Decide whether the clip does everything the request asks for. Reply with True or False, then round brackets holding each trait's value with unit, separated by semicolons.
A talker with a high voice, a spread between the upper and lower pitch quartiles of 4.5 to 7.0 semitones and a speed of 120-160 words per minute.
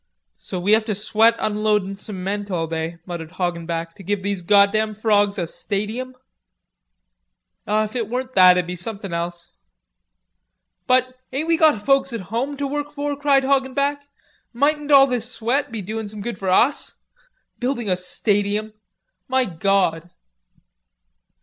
True (215 Hz; 5.3 semitones; 150 wpm)